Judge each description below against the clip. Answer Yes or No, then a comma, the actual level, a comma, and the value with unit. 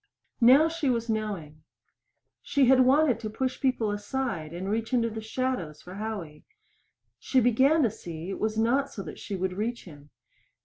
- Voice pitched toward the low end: No, high, 220 Hz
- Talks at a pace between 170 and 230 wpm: Yes, average, 175 wpm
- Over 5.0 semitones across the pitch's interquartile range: Yes, wide, 5.4 semitones